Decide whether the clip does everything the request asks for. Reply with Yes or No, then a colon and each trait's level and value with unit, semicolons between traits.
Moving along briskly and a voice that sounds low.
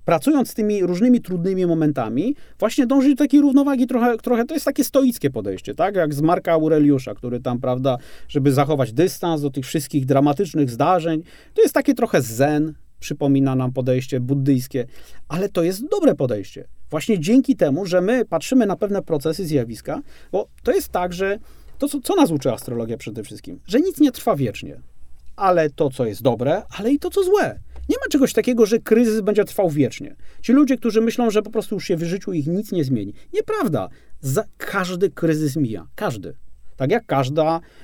No: fast, 190 wpm; medium, 180 Hz